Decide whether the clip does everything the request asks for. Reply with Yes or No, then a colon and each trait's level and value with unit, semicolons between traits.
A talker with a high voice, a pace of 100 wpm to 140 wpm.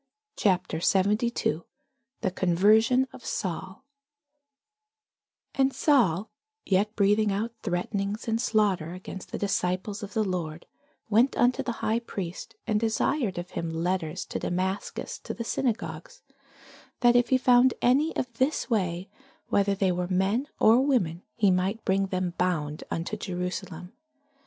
Yes: high, 200 Hz; slow, 135 wpm